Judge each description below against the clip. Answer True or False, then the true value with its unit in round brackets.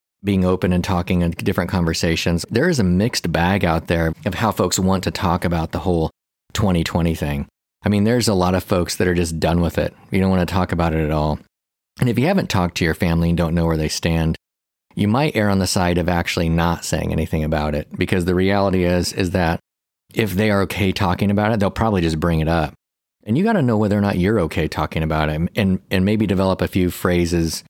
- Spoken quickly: True (245 wpm)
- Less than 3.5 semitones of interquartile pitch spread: True (2.8 semitones)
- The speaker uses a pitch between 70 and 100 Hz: True (90 Hz)